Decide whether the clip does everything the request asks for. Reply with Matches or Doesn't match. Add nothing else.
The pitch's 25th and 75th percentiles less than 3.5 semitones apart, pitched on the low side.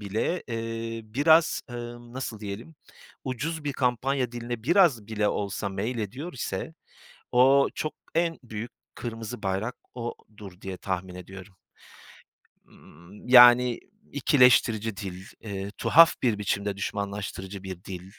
Doesn't match